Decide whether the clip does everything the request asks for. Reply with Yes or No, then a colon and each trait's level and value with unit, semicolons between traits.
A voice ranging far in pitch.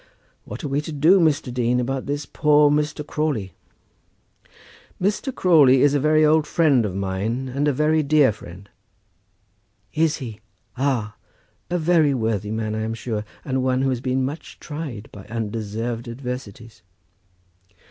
No: average, 4.9 semitones